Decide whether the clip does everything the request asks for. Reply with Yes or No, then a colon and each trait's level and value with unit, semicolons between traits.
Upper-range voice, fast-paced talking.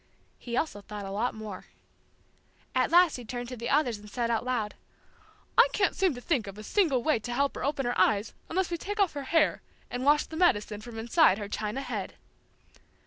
Yes: high, 245 Hz; fast, 215 wpm